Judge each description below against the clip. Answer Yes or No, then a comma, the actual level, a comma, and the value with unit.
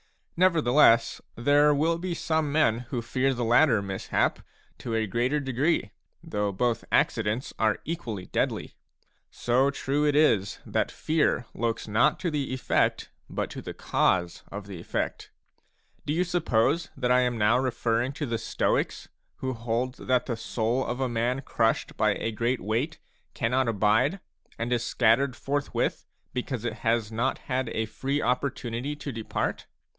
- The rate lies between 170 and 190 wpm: No, average, 160 wpm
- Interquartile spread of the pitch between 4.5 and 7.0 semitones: No, average, 3.7 semitones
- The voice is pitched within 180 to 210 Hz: No, low, 125 Hz